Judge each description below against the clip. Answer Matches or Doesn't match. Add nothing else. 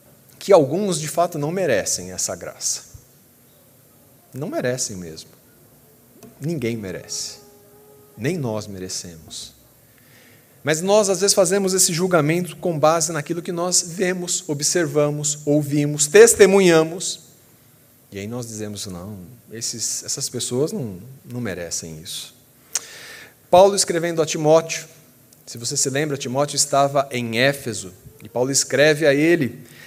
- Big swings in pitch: Matches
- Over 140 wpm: Doesn't match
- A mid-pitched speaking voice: Matches